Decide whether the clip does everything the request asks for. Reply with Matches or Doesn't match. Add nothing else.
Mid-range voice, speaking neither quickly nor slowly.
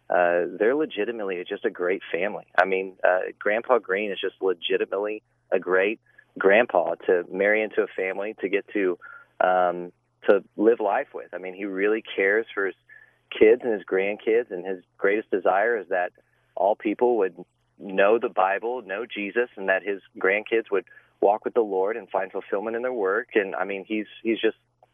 Doesn't match